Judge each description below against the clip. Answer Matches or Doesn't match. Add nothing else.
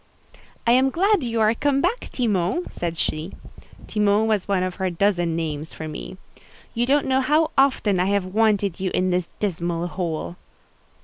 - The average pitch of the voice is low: Doesn't match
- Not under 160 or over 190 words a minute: Matches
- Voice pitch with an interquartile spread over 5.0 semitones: Matches